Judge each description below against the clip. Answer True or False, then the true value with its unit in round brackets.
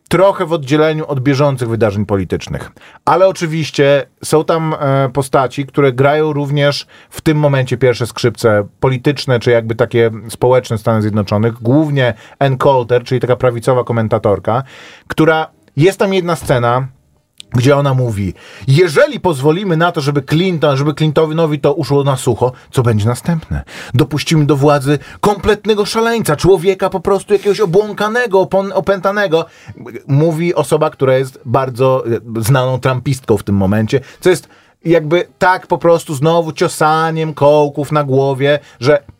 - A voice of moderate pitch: True (145 Hz)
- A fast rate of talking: False (140 wpm)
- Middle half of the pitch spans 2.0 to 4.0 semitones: False (4.7 semitones)